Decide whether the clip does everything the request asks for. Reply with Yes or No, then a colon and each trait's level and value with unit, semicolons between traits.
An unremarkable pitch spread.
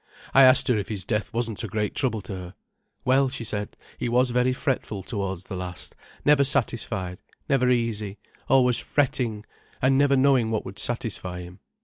Yes: average, 4.4 semitones